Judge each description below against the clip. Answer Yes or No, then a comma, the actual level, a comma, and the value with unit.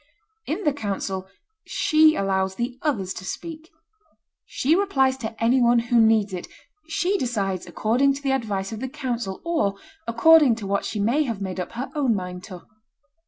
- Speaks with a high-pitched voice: Yes, high, 235 Hz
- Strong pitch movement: Yes, wide, 6.0 semitones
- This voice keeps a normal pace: Yes, average, 175 wpm